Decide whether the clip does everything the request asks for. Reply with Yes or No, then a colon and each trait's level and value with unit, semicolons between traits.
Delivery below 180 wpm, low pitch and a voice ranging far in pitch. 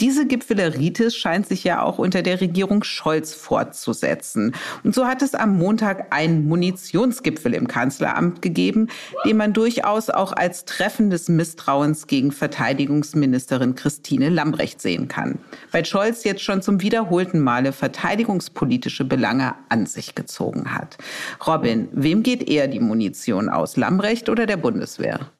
No: average, 140 wpm; high, 190 Hz; wide, 6.0 semitones